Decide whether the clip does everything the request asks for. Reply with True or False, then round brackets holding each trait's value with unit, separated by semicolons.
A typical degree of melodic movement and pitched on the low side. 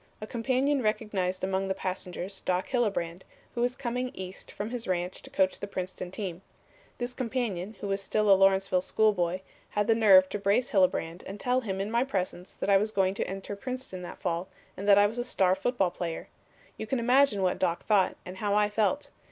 False (3.5 semitones; 200 Hz)